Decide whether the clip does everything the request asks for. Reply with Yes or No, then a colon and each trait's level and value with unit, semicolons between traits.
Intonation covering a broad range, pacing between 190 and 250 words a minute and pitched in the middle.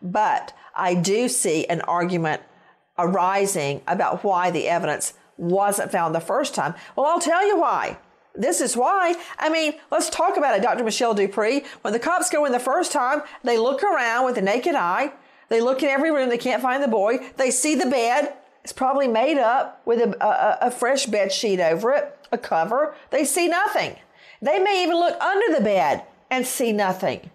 No: wide, 6.9 semitones; average, 195 wpm; very high, 255 Hz